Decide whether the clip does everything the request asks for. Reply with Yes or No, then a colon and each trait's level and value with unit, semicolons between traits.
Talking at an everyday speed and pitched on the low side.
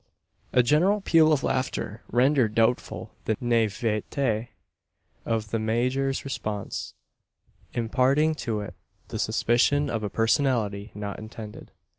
No: slow, 115 wpm; low, 120 Hz